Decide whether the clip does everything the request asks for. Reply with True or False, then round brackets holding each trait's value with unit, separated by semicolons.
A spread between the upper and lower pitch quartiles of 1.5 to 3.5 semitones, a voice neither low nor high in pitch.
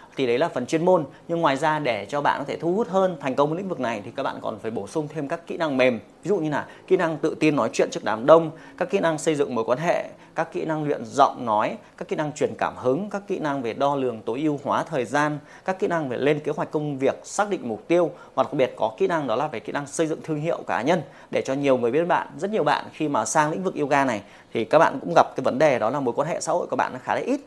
True (3.1 semitones; 155 Hz)